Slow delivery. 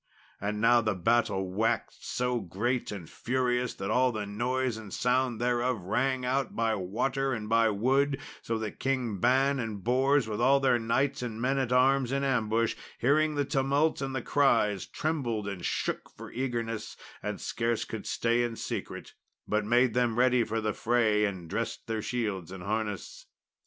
No: average, 175 wpm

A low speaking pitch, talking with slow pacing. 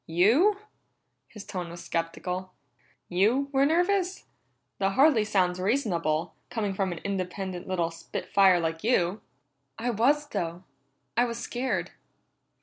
No: high, 195 Hz; slow, 130 wpm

